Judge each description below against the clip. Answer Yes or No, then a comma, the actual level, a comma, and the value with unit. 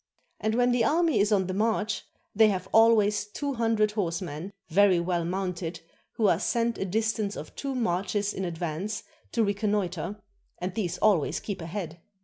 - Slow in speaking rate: No, average, 170 wpm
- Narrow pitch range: No, average, 3.6 semitones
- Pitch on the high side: Yes, high, 205 Hz